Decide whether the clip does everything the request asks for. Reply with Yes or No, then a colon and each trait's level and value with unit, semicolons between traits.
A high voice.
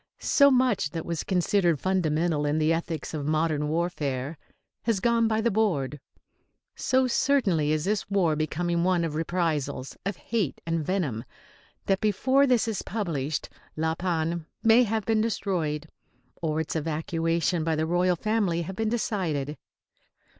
No: medium, 170 Hz